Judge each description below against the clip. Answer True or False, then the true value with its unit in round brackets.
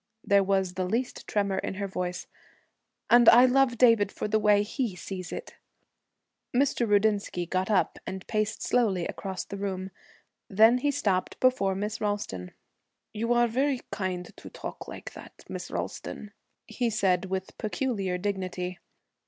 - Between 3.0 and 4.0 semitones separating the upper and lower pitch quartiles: True (3.5 semitones)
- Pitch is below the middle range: False (205 Hz)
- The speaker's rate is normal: True (155 wpm)